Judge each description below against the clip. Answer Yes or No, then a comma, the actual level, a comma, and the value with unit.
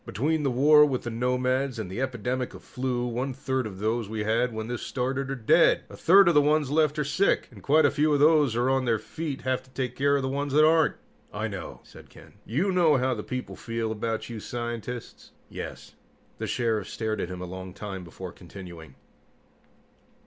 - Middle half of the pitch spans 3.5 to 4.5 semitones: Yes, average, 4.2 semitones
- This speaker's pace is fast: Yes, fast, 215 wpm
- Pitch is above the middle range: No, low, 125 Hz